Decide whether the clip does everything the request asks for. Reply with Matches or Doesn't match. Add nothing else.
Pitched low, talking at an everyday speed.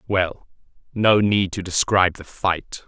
Matches